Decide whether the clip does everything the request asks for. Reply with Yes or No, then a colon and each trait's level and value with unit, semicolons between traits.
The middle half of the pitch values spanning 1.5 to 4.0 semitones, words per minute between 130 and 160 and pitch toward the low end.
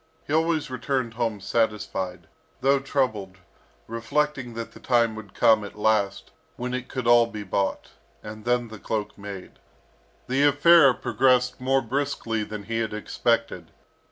Yes: average, 3.5 semitones; average, 150 wpm; low, 115 Hz